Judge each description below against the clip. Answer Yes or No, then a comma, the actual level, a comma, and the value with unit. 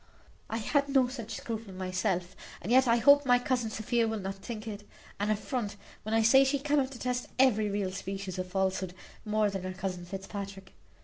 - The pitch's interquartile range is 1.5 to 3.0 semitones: No, average, 4.3 semitones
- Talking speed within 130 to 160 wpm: No, average, 190 wpm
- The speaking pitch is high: Yes, high, 215 Hz